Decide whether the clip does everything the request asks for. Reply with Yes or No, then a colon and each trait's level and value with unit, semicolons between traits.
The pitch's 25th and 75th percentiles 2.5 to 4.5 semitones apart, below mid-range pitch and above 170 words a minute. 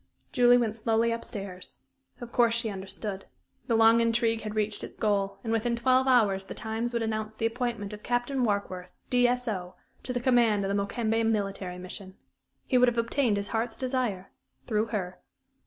No: average, 3.0 semitones; high, 225 Hz; average, 180 wpm